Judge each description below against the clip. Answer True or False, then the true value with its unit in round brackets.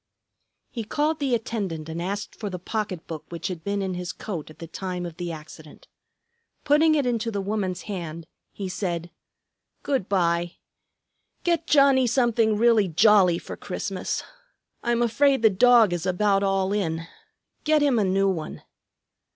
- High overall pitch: True (200 Hz)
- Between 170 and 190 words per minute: False (160 wpm)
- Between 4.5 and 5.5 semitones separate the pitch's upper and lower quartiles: True (5.1 semitones)